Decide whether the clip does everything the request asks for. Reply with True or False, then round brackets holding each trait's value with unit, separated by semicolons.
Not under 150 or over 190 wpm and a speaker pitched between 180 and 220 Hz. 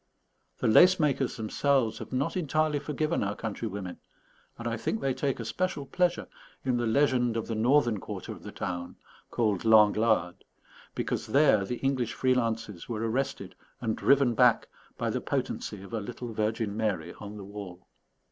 False (170 wpm; 115 Hz)